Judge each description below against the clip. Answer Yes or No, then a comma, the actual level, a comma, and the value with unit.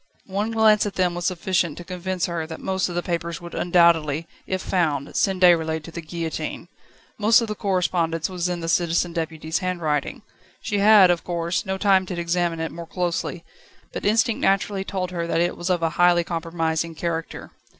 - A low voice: No, medium, 175 Hz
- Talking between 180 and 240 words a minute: Yes, average, 190 wpm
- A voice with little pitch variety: Yes, narrow, 2.1 semitones